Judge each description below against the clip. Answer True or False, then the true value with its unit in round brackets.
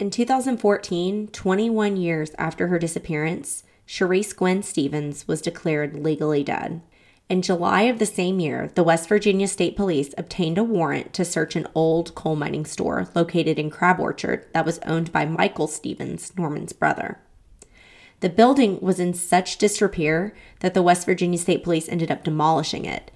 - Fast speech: False (165 wpm)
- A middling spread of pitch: True (3.3 semitones)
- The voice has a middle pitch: True (175 Hz)